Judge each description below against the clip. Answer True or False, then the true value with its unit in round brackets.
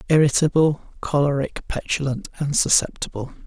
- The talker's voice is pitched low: False (145 Hz)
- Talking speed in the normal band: False (85 wpm)